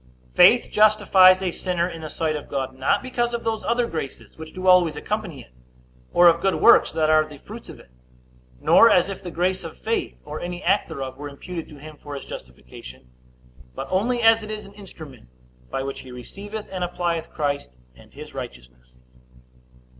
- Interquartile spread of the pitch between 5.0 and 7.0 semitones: Yes, wide, 5.5 semitones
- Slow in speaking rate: No, average, 195 wpm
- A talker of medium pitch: Yes, medium, 170 Hz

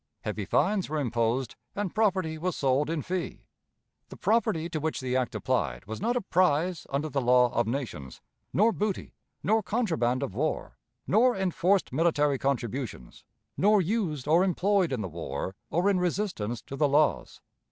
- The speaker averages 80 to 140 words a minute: No, average, 165 wpm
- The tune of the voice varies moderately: No, wide, 6.8 semitones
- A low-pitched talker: No, medium, 155 Hz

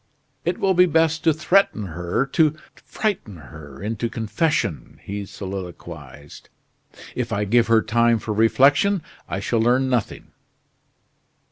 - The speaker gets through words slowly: Yes, slow, 130 wpm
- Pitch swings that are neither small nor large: No, wide, 8.0 semitones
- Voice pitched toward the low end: Yes, low, 115 Hz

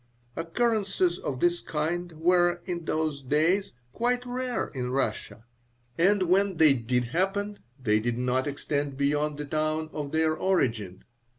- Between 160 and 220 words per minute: No, average, 140 wpm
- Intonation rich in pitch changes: No, average, 4.9 semitones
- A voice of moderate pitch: Yes, medium, 160 Hz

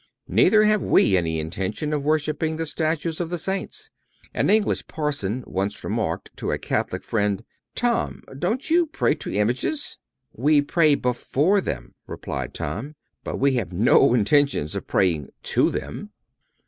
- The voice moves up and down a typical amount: No, wide, 8.7 semitones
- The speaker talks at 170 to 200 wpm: No, average, 150 wpm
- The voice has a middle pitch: Yes, medium, 145 Hz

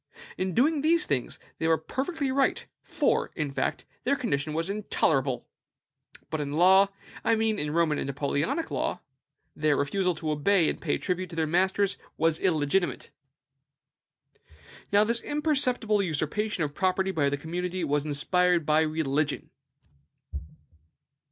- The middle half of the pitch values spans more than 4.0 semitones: Yes, average, 5.2 semitones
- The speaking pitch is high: No, medium, 170 Hz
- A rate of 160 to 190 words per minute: No, average, 140 wpm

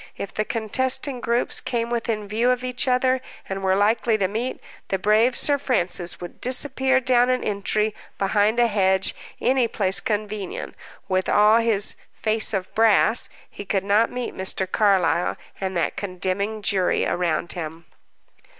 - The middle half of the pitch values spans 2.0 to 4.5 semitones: Yes, average, 3.8 semitones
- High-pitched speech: Yes, high, 215 Hz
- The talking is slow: No, average, 155 wpm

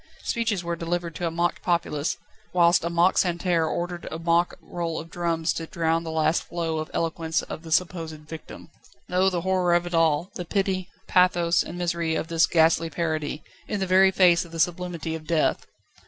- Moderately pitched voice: Yes, medium, 170 Hz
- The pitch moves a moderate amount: No, narrow, 1.5 semitones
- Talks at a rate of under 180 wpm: No, average, 195 wpm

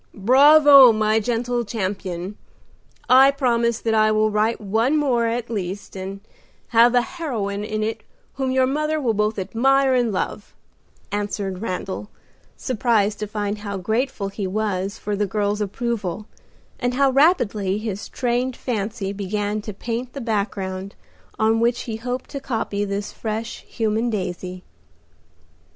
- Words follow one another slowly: No, average, 145 wpm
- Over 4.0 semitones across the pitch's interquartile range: No, average, 3.4 semitones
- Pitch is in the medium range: No, high, 220 Hz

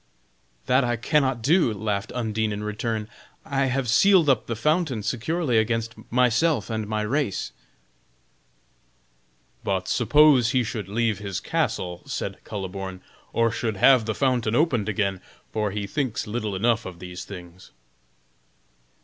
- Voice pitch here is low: Yes, low, 110 Hz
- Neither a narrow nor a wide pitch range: Yes, average, 3.7 semitones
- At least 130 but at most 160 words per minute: Yes, average, 140 wpm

